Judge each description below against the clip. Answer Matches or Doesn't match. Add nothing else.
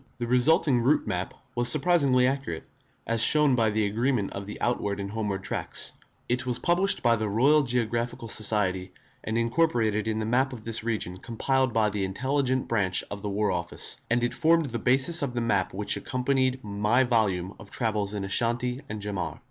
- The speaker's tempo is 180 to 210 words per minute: Matches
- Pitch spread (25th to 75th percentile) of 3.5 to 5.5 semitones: Matches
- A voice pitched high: Doesn't match